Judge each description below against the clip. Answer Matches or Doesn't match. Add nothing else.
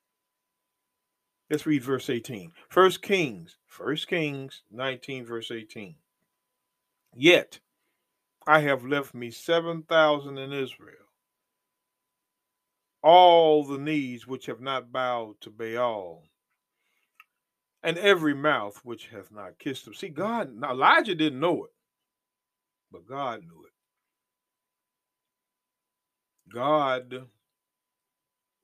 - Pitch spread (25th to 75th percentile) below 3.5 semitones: Doesn't match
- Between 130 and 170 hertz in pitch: Matches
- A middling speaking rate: Doesn't match